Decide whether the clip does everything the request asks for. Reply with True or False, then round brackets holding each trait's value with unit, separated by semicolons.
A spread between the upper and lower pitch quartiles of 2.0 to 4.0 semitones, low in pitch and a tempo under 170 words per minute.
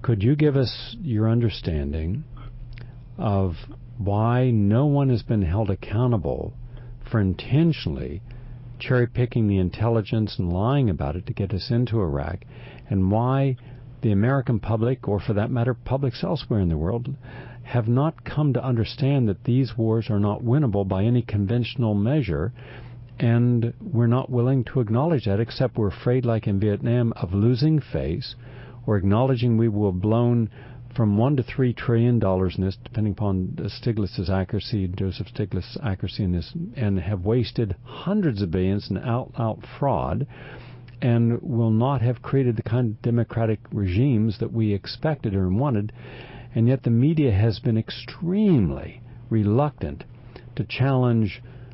True (3.1 semitones; 120 Hz; 155 wpm)